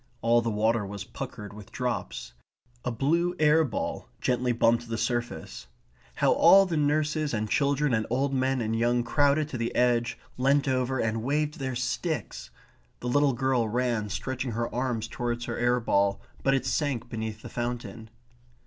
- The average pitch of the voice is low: Yes, low, 125 Hz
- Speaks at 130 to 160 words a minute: No, average, 170 wpm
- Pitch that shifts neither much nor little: Yes, average, 3.1 semitones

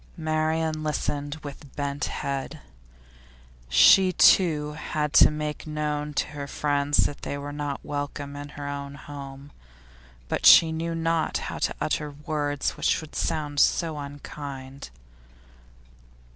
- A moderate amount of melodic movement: No, narrow, 1.5 semitones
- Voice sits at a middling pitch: Yes, medium, 145 Hz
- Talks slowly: Yes, slow, 130 wpm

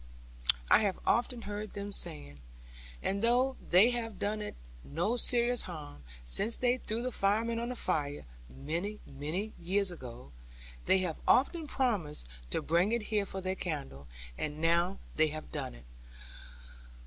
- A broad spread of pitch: Yes, wide, 6.9 semitones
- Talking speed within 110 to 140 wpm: No, average, 155 wpm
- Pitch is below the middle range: No, high, 195 Hz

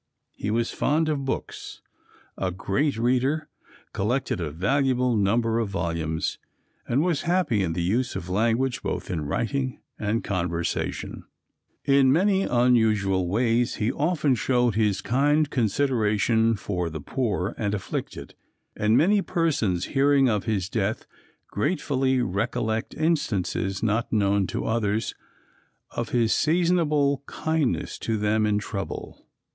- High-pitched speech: No, low, 115 Hz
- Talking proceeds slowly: Yes, slow, 130 wpm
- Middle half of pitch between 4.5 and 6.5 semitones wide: Yes, average, 5.3 semitones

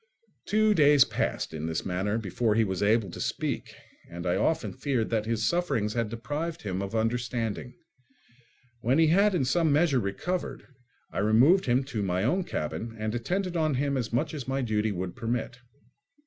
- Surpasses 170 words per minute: Yes, average, 180 wpm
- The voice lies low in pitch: Yes, low, 120 Hz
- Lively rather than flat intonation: Yes, wide, 5.9 semitones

